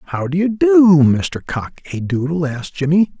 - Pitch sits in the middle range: Yes, medium, 165 Hz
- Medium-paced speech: Yes, average, 190 wpm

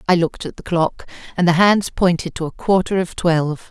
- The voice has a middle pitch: Yes, medium, 175 Hz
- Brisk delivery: Yes, fast, 225 wpm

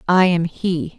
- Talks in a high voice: No, medium, 175 Hz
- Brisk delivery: No, average, 185 wpm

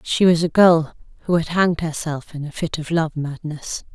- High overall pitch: No, medium, 160 Hz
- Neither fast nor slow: No, fast, 215 wpm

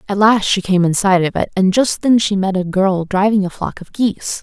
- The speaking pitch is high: Yes, high, 195 Hz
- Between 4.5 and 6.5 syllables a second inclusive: Yes, 5.2 syllables/s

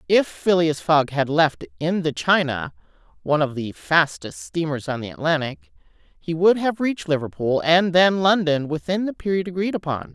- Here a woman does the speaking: Yes, female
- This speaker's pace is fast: No, average, 170 wpm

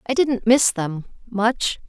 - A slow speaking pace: Yes, slow, 130 wpm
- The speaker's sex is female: Yes, female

